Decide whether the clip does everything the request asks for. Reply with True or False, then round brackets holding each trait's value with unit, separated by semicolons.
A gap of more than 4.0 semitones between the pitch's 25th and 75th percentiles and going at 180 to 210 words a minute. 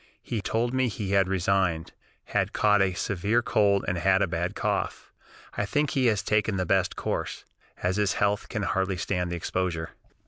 False (2.6 semitones; 185 wpm)